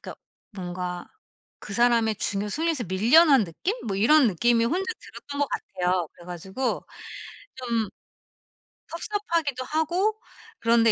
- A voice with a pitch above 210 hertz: Yes, high, 235 Hz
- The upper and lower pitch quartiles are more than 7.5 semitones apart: Yes, wide, 8.1 semitones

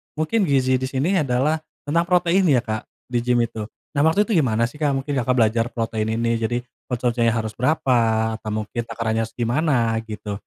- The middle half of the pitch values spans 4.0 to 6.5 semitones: Yes, average, 4.4 semitones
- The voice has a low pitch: Yes, low, 120 Hz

